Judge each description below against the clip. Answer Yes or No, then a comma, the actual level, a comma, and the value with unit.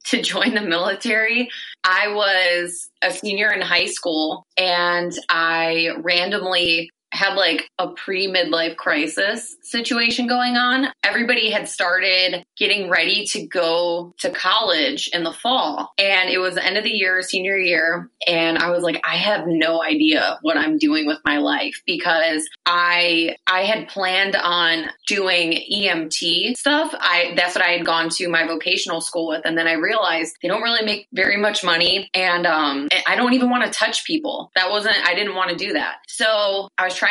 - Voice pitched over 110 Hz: Yes, medium, 185 Hz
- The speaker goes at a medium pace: Yes, average, 180 wpm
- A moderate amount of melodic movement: Yes, average, 3.9 semitones